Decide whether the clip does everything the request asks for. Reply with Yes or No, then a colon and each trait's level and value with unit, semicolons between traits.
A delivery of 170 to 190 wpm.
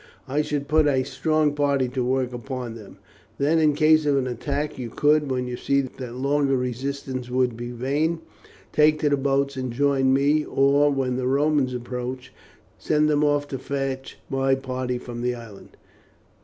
Yes: average, 180 wpm